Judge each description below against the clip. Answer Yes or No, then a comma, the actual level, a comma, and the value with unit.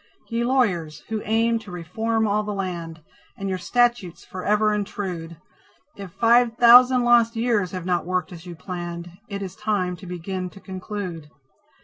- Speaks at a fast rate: No, average, 160 wpm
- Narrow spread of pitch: No, average, 4.1 semitones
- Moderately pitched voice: No, high, 195 Hz